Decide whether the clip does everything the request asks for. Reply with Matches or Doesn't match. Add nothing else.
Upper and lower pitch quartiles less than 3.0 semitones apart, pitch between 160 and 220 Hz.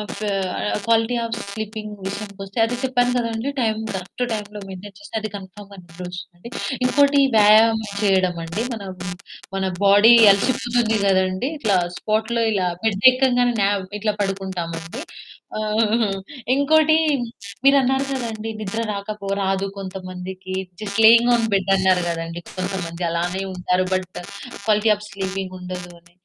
Doesn't match